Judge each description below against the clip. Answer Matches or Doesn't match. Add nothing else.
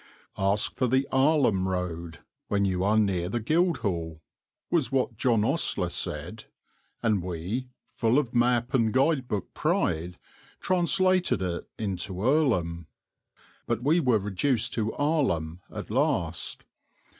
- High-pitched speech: Doesn't match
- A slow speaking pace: Matches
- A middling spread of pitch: Doesn't match